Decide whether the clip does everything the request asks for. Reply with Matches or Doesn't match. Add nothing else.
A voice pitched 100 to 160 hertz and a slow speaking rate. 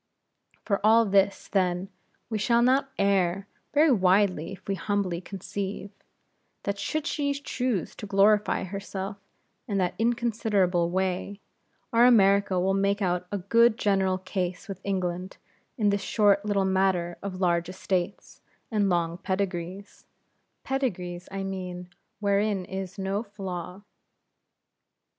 Doesn't match